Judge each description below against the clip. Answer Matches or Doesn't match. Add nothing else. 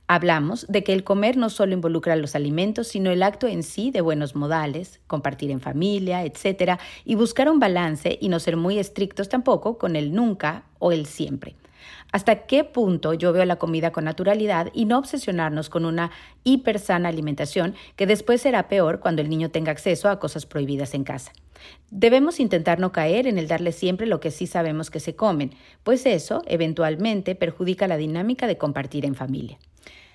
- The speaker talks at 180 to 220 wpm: Matches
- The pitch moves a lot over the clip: Doesn't match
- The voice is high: Doesn't match